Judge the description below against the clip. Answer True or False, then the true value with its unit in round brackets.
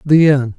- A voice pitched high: False (140 Hz)